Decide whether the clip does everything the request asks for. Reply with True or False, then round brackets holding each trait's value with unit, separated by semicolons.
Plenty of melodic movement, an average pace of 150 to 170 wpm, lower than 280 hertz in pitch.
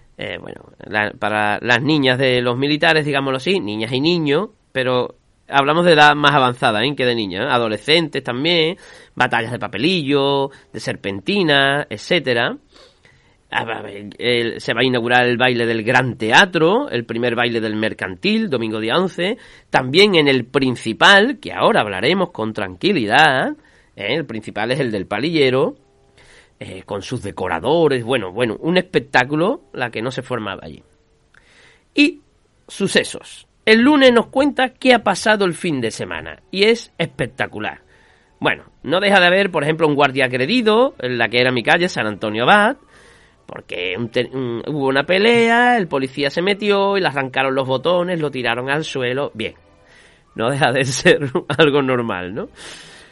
True (6.3 semitones; 165 wpm; 135 Hz)